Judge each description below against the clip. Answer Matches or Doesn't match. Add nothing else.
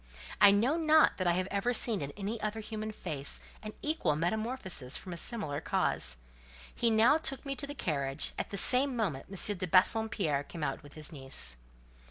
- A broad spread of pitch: Matches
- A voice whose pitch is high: Matches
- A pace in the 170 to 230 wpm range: Matches